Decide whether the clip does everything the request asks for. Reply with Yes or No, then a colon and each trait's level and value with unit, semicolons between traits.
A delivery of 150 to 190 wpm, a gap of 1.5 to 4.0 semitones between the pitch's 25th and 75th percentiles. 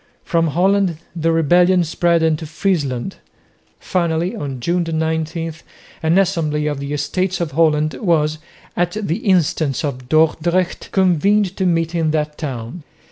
No: slow, 135 wpm; average, 2.7 semitones